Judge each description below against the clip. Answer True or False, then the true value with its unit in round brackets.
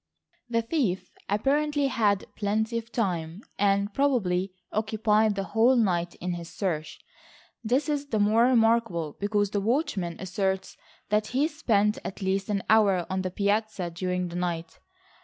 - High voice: True (205 Hz)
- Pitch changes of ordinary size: True (3.6 semitones)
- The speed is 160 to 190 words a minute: False (150 wpm)